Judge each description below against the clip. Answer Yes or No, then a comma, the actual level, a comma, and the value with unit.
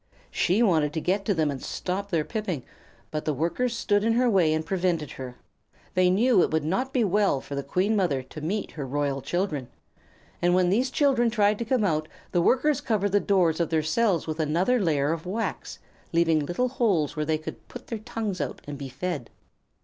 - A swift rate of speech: Yes, fast, 210 wpm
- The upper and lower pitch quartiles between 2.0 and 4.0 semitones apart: No, wide, 5.6 semitones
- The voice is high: No, medium, 180 Hz